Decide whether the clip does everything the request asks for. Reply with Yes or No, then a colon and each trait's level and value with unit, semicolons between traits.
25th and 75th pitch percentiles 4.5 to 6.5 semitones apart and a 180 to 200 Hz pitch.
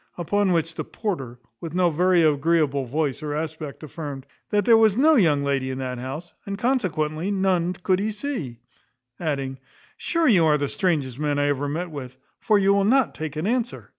No: wide, 5.5 semitones; medium, 160 Hz